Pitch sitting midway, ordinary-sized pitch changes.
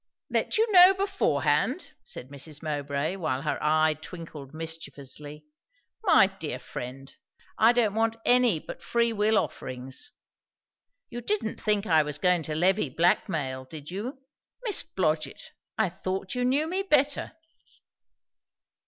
No: medium, 175 Hz; wide, 7.8 semitones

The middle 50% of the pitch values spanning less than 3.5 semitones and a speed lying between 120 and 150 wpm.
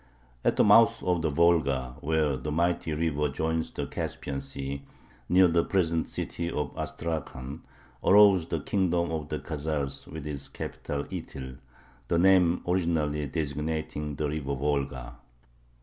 Yes: average, 3.0 semitones; average, 140 wpm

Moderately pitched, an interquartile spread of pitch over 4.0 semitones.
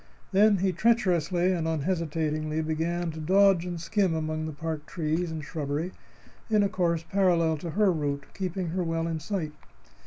No: medium, 165 Hz; average, 2.8 semitones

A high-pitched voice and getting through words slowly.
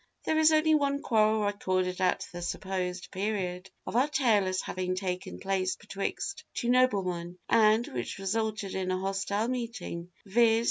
No: high, 200 Hz; average, 155 wpm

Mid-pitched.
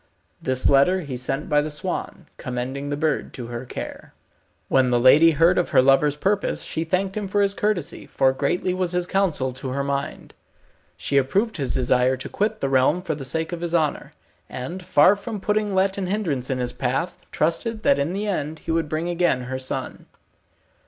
Yes: medium, 155 Hz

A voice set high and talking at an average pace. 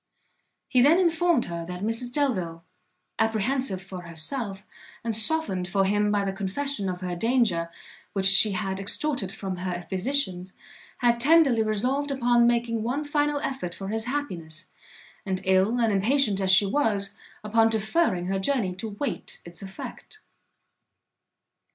Yes: high, 215 Hz; average, 145 wpm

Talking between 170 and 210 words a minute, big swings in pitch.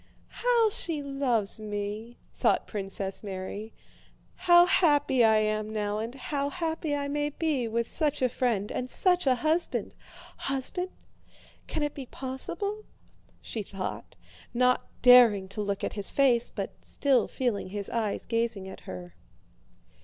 No: average, 145 wpm; wide, 5.7 semitones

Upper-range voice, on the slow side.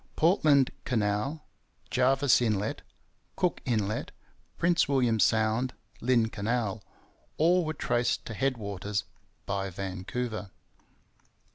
No: low, 120 Hz; slow, 100 wpm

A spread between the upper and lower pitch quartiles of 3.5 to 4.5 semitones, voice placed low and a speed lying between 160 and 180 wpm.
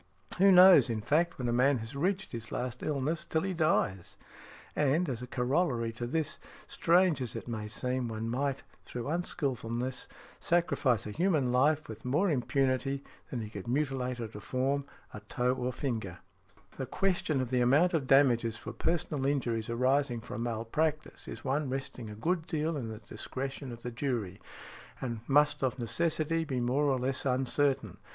Yes: average, 3.9 semitones; low, 130 Hz; average, 175 wpm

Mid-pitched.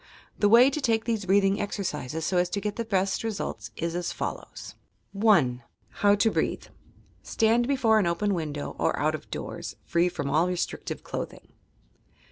No: high, 195 Hz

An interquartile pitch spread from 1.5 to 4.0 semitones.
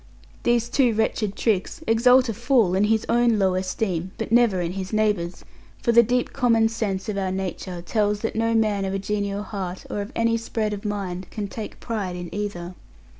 Yes: average, 3.1 semitones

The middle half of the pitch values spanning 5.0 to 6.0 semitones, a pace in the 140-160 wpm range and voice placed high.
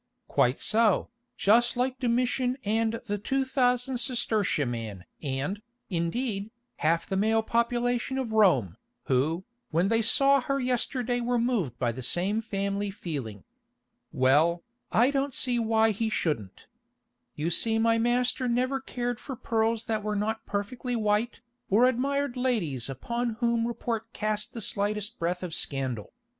Yes: average, 5.3 semitones; average, 145 wpm; high, 225 Hz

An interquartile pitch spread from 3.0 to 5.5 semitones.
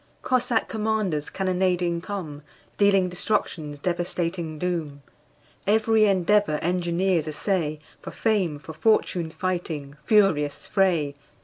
Yes: average, 4.3 semitones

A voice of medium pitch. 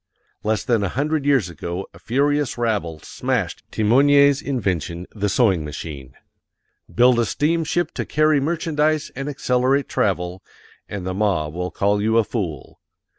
No: low, 115 Hz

